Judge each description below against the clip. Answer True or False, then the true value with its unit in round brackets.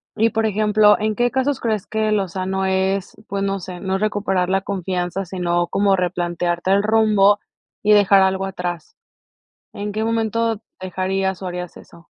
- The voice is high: True (195 Hz)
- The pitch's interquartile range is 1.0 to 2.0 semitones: False (2.4 semitones)